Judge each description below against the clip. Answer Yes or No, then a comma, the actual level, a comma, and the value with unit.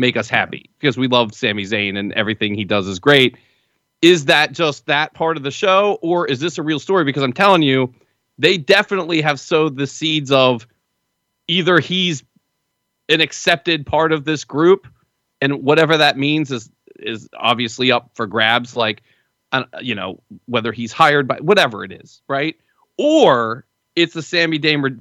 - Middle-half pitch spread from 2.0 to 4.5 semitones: No, average, 5.0 semitones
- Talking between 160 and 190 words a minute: Yes, average, 175 wpm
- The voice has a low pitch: No, medium, 145 Hz